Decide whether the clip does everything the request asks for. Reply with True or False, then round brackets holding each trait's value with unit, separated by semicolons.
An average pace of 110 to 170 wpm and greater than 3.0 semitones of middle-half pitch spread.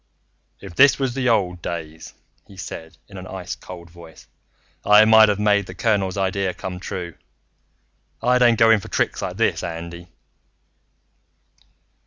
True (150 wpm; 3.9 semitones)